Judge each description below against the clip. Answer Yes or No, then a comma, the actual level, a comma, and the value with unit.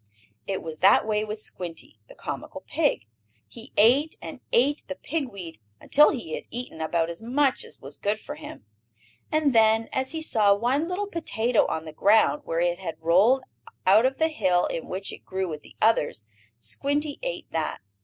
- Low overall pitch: No, high, 220 Hz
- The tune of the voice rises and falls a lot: Yes, wide, 8.0 semitones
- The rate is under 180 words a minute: No, average, 190 wpm